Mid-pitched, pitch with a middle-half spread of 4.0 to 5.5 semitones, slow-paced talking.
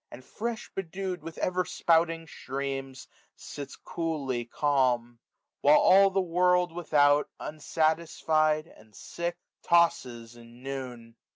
Yes: medium, 155 Hz; average, 4.8 semitones; slow, 110 wpm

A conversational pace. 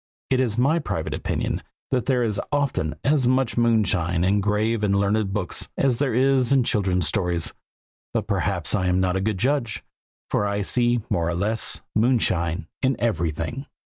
Yes: average, 170 wpm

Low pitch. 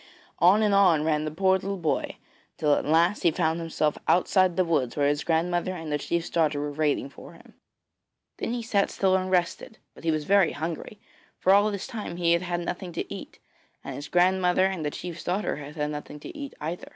No: medium, 170 Hz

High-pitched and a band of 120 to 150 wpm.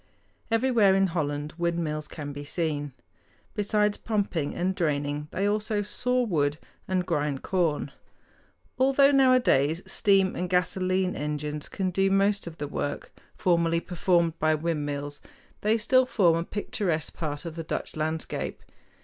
No: medium, 170 Hz; average, 140 wpm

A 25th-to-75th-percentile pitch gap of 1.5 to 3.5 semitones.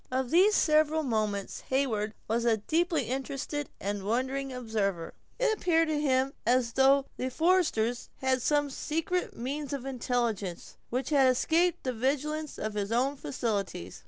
No: average, 4.6 semitones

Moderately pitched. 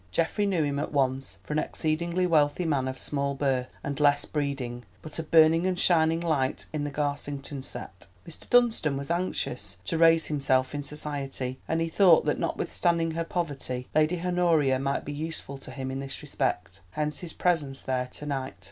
Yes: medium, 145 Hz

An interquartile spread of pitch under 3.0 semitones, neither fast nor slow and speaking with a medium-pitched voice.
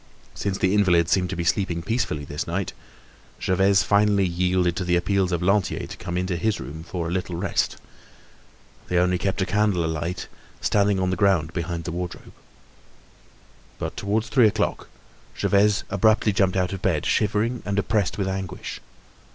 No: narrow, 2.4 semitones; average, 170 wpm; very low, 95 Hz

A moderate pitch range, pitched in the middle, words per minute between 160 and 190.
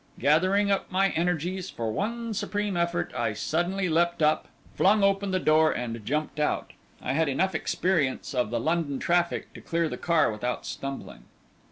Yes: average, 5.0 semitones; medium, 170 Hz; average, 170 wpm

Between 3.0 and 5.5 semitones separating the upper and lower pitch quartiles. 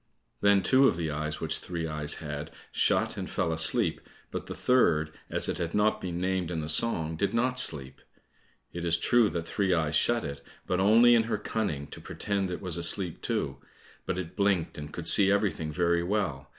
Yes: average, 4.4 semitones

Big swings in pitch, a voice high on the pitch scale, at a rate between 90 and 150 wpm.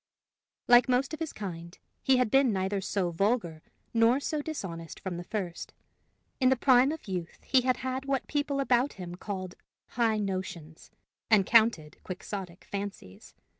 No: wide, 6.0 semitones; high, 215 Hz; average, 165 wpm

